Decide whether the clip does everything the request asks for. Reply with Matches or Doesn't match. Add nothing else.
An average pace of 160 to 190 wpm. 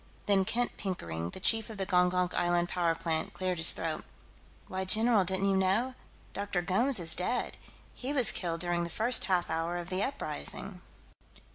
Matches